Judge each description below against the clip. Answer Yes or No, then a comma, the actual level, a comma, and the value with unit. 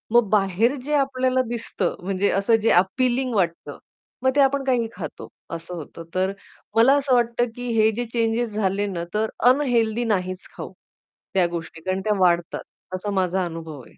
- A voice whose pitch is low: No, high, 215 Hz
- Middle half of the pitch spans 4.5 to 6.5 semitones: Yes, average, 4.8 semitones